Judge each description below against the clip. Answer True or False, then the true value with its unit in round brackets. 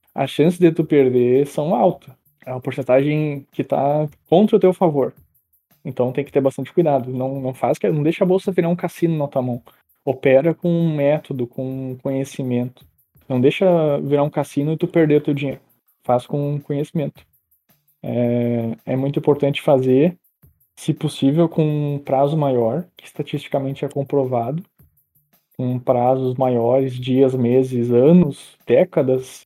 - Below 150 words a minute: False (160 wpm)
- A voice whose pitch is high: False (140 Hz)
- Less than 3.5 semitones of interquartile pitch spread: True (3.1 semitones)